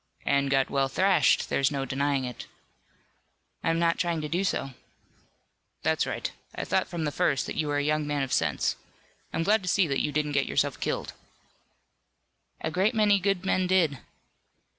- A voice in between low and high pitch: Yes, medium, 150 Hz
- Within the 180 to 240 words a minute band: Yes, average, 185 wpm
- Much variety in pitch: No, average, 4.7 semitones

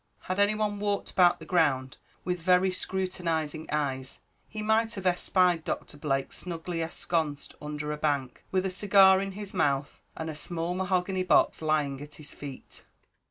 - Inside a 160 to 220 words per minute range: Yes, average, 165 wpm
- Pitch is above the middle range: No, medium, 175 Hz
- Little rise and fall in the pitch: No, average, 4.1 semitones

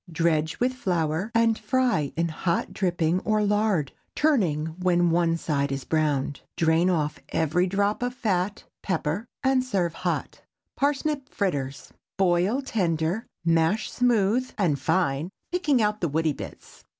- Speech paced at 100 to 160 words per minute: Yes, average, 140 wpm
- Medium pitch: Yes, medium, 180 Hz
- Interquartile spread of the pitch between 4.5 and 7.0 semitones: Yes, average, 5.3 semitones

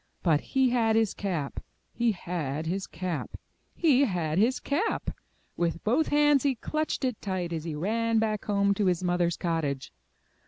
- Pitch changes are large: Yes, wide, 5.9 semitones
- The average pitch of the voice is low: No, high, 195 Hz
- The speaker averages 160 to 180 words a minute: Yes, average, 165 wpm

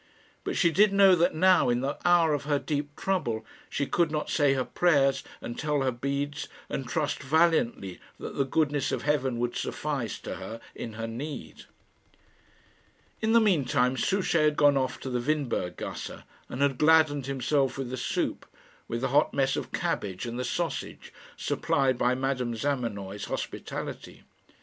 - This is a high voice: No, medium, 140 Hz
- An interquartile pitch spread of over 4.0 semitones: No, average, 3.7 semitones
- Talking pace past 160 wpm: Yes, average, 175 wpm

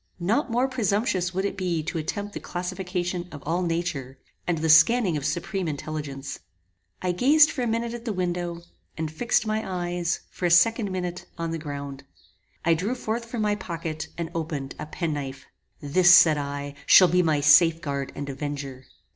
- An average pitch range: Yes, average, 4.2 semitones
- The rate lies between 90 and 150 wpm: No, average, 180 wpm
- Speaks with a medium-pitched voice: Yes, medium, 175 Hz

